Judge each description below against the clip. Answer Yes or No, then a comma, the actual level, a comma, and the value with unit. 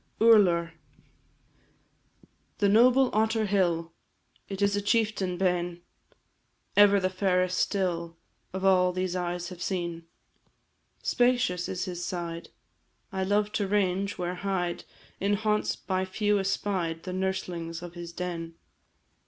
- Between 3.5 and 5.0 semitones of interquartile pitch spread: No, narrow, 2.6 semitones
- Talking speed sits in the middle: No, slow, 125 wpm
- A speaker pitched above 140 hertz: Yes, medium, 185 Hz